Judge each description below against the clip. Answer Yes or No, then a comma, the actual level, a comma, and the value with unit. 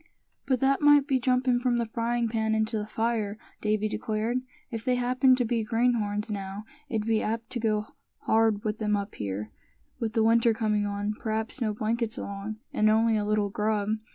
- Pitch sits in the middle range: No, high, 220 Hz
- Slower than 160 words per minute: No, average, 190 wpm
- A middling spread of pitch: No, narrow, 2.0 semitones